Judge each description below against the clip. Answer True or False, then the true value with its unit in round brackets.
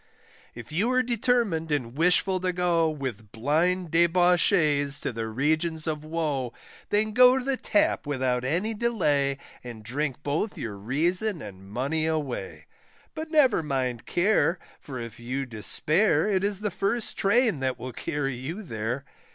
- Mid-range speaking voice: True (155 Hz)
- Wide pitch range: True (6.7 semitones)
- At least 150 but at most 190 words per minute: True (155 wpm)